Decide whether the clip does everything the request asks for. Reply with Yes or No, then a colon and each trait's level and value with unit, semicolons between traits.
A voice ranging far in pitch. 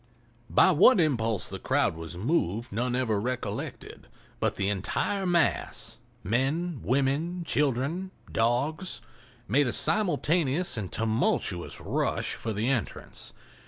Yes: wide, 6.1 semitones